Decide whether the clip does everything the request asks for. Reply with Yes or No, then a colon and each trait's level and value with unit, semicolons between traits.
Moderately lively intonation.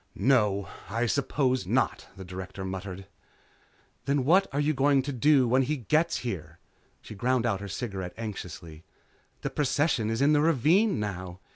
No: wide, 6.7 semitones